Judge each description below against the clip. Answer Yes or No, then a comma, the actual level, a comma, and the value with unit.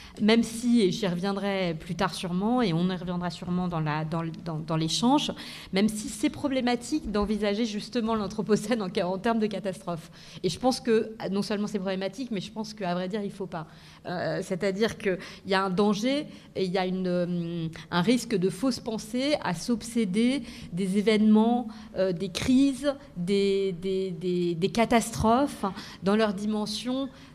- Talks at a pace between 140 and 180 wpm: Yes, average, 170 wpm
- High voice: Yes, high, 200 Hz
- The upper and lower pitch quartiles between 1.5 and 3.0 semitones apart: No, average, 3.6 semitones